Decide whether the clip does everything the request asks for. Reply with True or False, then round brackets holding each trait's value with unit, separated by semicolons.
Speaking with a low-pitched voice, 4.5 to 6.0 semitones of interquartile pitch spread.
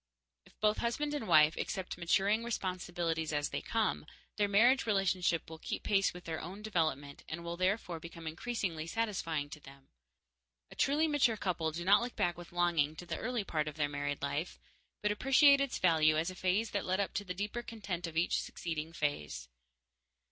False (180 Hz; 4.8 semitones)